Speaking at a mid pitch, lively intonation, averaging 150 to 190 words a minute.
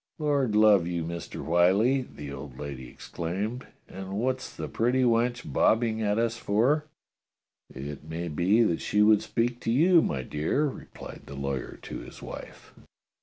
No: low, 105 Hz; wide, 6.8 semitones; average, 165 wpm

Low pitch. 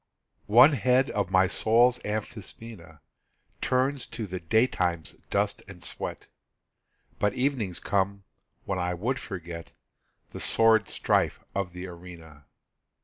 Yes: low, 100 Hz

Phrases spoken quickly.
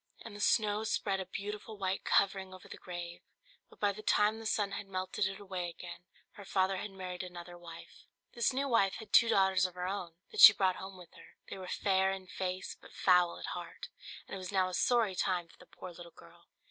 Yes: fast, 230 wpm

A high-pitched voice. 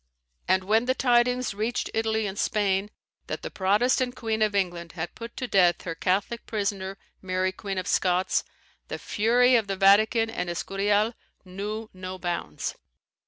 Yes: high, 205 Hz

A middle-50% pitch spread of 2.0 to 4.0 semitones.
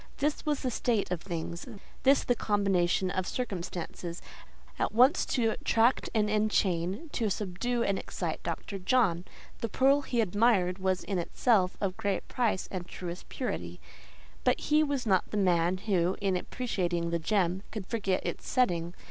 No: average, 4.8 semitones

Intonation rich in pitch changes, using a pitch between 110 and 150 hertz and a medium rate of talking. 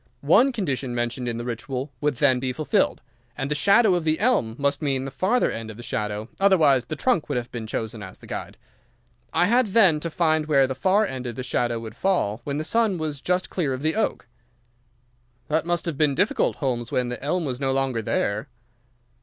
No: wide, 6.0 semitones; medium, 140 Hz; fast, 220 wpm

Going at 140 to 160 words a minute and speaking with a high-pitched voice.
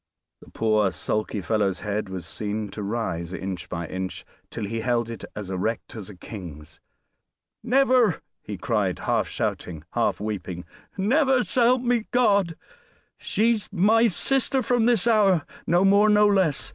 No: average, 150 wpm; low, 115 Hz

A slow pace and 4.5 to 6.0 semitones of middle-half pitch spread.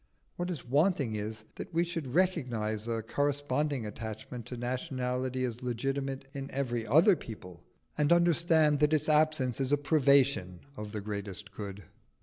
No: average, 150 wpm; average, 5.1 semitones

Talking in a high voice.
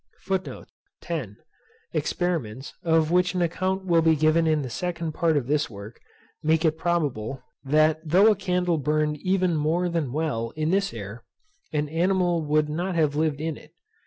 No: medium, 160 Hz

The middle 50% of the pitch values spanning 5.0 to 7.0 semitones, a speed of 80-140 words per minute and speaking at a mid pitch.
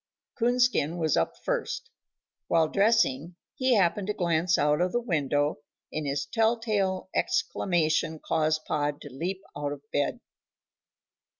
Yes: wide, 5.4 semitones; slow, 135 wpm; medium, 165 Hz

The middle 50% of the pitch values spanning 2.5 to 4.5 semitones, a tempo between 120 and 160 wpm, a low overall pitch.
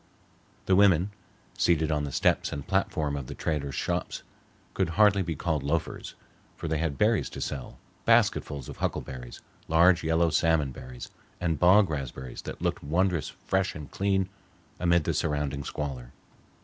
Yes: average, 4.1 semitones; average, 155 wpm; very low, 80 Hz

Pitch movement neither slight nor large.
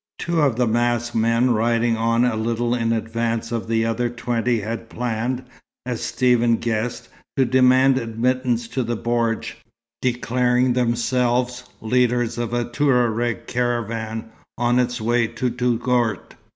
No: narrow, 1.4 semitones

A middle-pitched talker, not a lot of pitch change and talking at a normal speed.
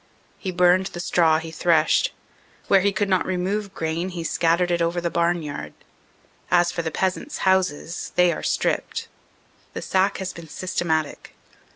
Yes: medium, 175 Hz; narrow, 2.2 semitones; average, 160 wpm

